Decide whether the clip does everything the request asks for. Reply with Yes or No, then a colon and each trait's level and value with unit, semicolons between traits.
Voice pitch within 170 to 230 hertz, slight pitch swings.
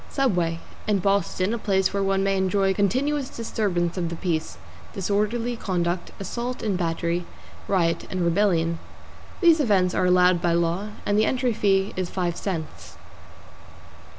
No: high, 190 Hz; average, 3.2 semitones